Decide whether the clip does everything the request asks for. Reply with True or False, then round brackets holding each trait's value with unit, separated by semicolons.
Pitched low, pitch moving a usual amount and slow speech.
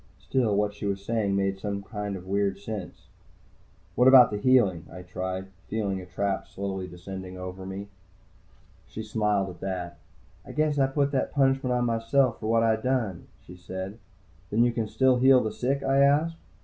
False (105 Hz; 4.6 semitones; 185 wpm)